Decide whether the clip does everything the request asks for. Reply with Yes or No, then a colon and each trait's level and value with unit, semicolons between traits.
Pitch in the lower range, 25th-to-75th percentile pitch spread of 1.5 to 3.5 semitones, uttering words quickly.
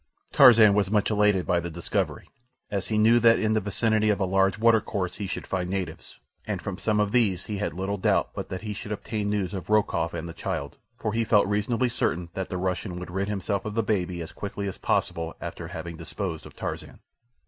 Yes: low, 100 Hz; average, 2.9 semitones; fast, 225 wpm